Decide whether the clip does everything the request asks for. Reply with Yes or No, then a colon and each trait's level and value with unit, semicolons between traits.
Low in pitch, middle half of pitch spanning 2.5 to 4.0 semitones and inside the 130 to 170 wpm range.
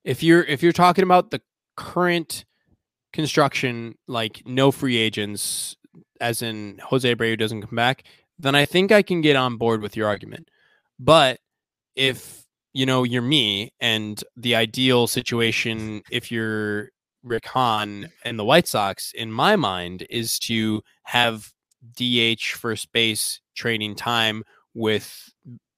Yes: low, 120 Hz; average, 3.2 semitones; average, 140 wpm